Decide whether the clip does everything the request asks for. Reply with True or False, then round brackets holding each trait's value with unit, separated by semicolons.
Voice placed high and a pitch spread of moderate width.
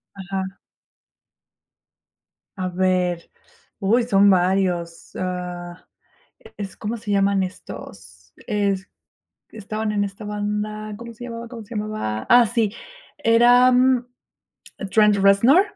True (205 Hz; 3.4 semitones)